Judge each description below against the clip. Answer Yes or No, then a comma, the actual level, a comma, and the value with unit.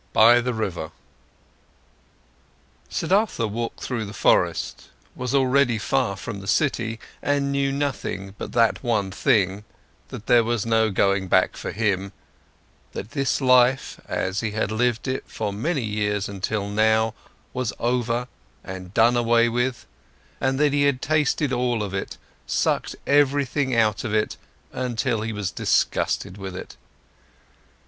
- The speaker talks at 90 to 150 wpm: Yes, average, 145 wpm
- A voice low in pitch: Yes, low, 115 Hz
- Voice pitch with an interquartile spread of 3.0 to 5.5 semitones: Yes, average, 3.9 semitones